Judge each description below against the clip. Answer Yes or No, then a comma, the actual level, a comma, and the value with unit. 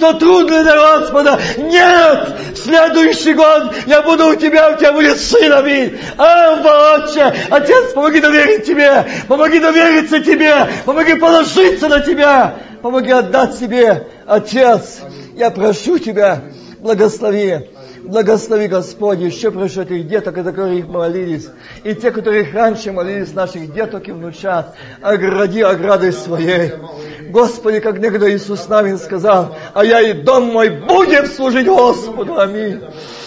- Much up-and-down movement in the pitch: Yes, wide, 7.6 semitones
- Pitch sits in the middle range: No, high, 230 Hz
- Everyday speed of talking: Yes, average, 135 wpm